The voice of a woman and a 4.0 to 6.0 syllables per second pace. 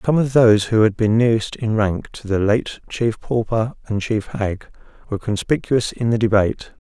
No: male; 5.1 syllables/s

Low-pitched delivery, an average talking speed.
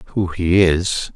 Yes: very low, 90 Hz; average, 155 wpm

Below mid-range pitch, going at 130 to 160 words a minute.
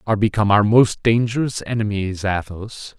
Yes: low, 105 Hz; average, 140 wpm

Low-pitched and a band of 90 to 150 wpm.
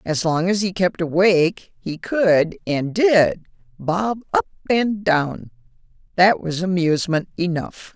No: medium, 175 Hz; slow, 135 wpm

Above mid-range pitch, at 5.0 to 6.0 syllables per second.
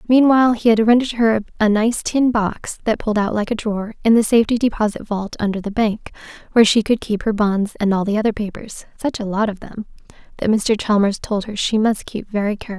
Yes: high, 215 Hz; 5.5 syllables/s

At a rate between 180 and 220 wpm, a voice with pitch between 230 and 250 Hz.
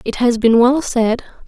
Yes: fast, 205 wpm; high, 240 Hz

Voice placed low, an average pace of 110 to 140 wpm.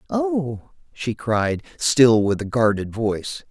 Yes: low, 120 Hz; slow, 135 wpm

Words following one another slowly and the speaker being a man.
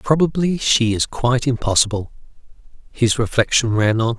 Yes: slow, 130 wpm; male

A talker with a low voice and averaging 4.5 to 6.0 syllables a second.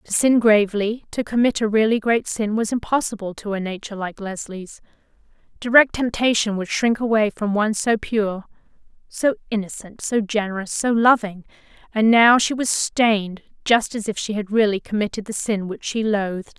No: high, 215 Hz; 5.2 syllables/s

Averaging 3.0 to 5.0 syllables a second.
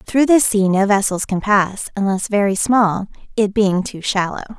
Yes: 4.6 syllables/s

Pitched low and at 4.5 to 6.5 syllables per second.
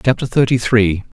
Yes: low, 115 Hz; 5.2 syllables/s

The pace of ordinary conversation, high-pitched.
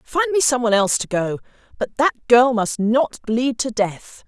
No: fast, 210 wpm; high, 240 Hz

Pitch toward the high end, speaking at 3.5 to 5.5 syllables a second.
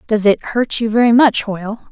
Yes: high, 220 Hz; 5.4 syllables/s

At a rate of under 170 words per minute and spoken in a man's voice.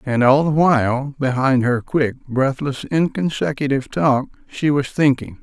Yes: average, 145 wpm; male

